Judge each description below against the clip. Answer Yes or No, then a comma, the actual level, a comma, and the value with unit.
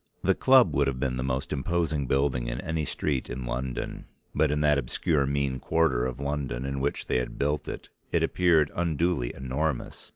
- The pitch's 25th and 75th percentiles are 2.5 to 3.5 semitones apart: Yes, average, 3.0 semitones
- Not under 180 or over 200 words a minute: Yes, average, 190 wpm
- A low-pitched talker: Yes, very low, 70 Hz